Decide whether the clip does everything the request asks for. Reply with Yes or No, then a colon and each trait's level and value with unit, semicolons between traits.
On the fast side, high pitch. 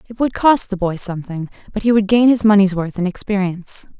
Yes: fast, 225 wpm; high, 200 Hz